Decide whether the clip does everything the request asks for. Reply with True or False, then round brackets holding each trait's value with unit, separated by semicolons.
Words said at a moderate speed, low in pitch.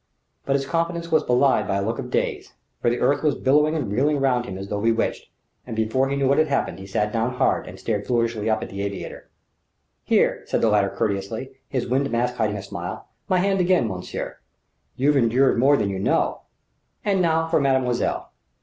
False (210 wpm; 125 Hz)